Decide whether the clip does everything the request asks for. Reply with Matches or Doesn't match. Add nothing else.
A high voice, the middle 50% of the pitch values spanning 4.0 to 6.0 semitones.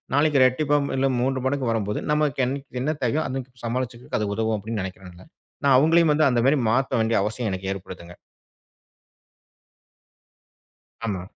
Doesn't match